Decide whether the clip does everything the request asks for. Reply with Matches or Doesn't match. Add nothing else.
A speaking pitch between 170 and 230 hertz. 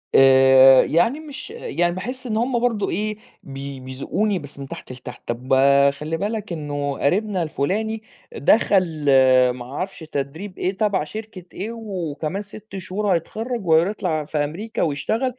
Matches